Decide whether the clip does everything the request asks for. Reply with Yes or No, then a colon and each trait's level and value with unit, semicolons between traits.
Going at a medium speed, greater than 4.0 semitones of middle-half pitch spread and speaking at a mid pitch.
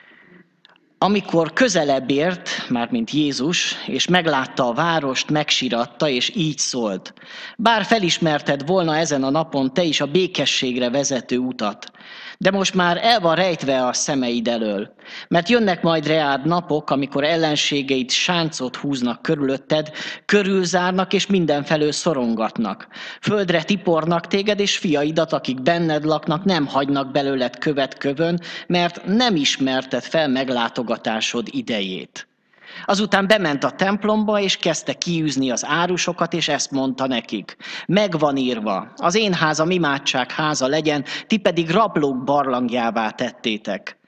Yes: average, 130 wpm; average, 5.0 semitones; medium, 155 Hz